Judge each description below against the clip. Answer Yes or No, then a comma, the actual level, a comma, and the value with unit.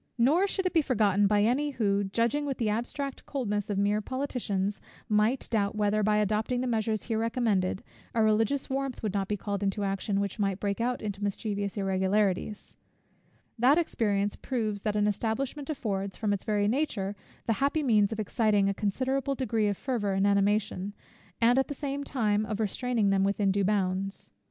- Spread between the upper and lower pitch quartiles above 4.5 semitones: No, average, 3.6 semitones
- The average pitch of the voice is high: Yes, high, 210 Hz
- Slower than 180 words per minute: No, average, 185 wpm